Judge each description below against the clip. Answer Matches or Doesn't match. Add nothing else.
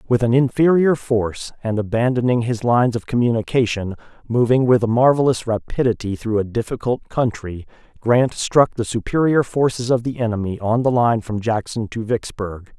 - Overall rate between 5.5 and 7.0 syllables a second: Doesn't match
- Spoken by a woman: Doesn't match